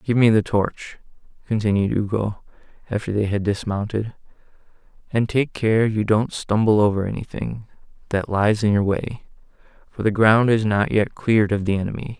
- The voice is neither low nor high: No, low, 105 Hz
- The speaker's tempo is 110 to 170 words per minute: Yes, average, 165 wpm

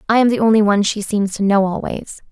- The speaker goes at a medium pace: No, fast, 260 wpm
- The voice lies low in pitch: No, high, 210 Hz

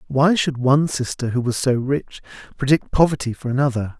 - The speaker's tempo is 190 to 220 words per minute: No, average, 180 wpm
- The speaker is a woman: No, male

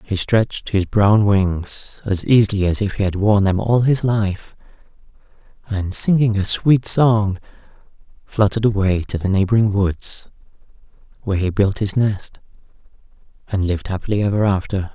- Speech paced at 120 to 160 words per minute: Yes, average, 150 wpm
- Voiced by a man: Yes, male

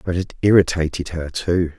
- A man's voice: Yes, male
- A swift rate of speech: No, average, 170 wpm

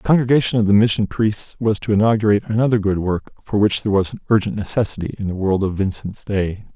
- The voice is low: Yes, low, 105 Hz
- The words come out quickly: Yes, fast, 220 wpm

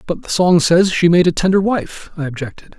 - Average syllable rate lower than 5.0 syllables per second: No, 5.4 syllables/s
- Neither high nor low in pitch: Yes, medium, 175 Hz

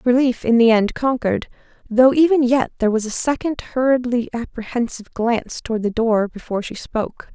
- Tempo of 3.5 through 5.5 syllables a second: No, 5.9 syllables/s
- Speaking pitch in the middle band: No, high, 240 Hz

